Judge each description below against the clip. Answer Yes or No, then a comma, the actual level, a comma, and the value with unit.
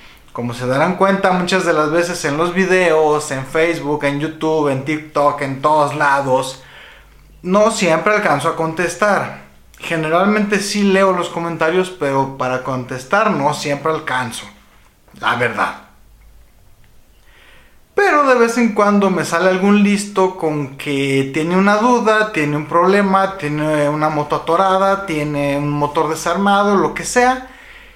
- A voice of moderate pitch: Yes, medium, 160 Hz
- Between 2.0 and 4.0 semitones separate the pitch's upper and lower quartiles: No, average, 5.1 semitones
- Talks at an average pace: Yes, average, 140 wpm